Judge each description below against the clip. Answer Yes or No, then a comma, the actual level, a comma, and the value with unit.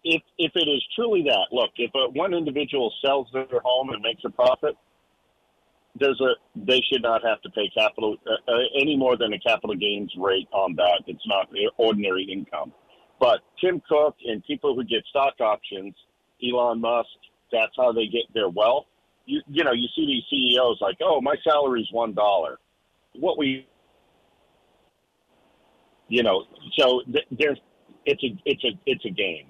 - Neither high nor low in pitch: No, low, 130 Hz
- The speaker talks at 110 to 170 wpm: No, average, 180 wpm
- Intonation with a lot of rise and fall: Yes, wide, 5.8 semitones